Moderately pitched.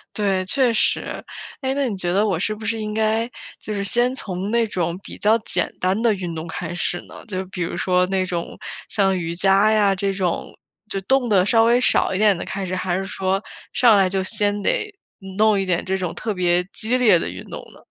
No: high, 195 Hz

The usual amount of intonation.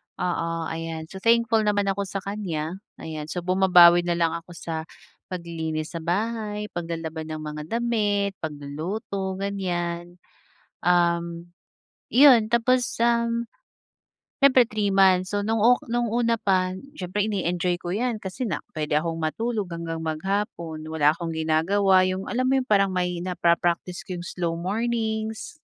Yes: average, 4.1 semitones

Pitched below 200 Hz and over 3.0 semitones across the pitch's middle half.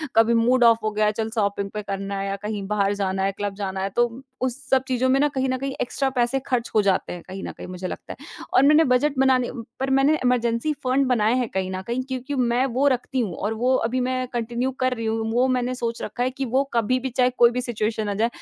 No: high, 240 Hz; average, 3.4 semitones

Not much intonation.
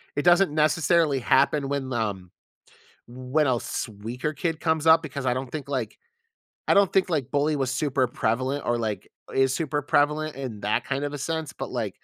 No: average, 3.3 semitones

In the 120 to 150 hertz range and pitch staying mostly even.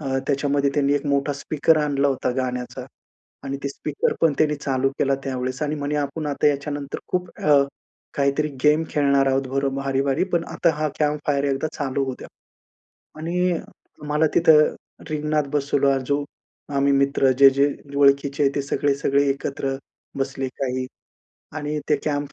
Yes: medium, 140 Hz; narrow, 1.5 semitones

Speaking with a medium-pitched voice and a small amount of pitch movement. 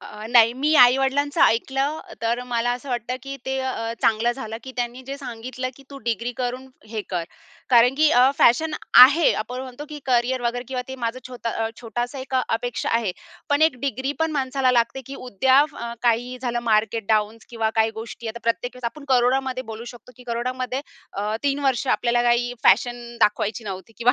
No: high, 245 Hz; narrow, 2.2 semitones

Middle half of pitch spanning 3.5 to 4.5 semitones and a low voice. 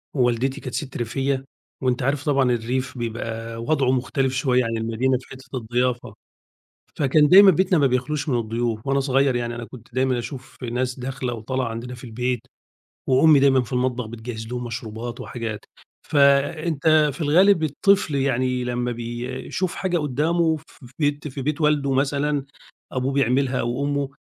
No: average, 2.8 semitones; low, 130 Hz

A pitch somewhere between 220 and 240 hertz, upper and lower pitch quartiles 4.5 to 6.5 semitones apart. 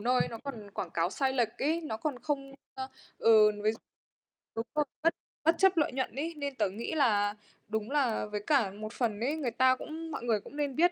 No: very high, 255 Hz; average, 5.2 semitones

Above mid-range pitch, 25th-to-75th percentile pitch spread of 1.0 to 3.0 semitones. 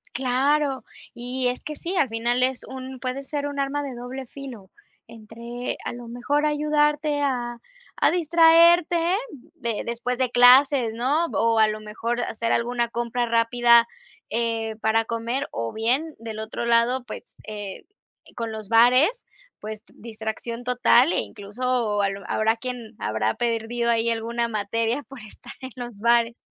Yes: high, 240 Hz; narrow, 2.5 semitones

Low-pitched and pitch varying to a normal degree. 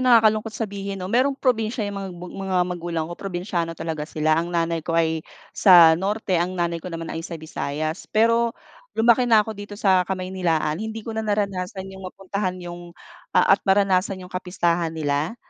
No: medium, 185 Hz; average, 3.6 semitones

